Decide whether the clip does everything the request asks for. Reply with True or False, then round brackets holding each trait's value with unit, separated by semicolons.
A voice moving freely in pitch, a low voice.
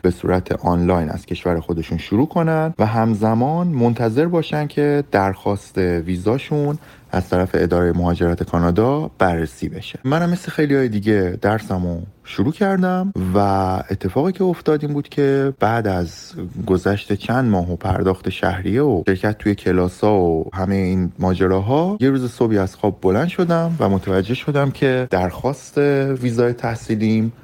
True (6.9 semitones; 105 Hz)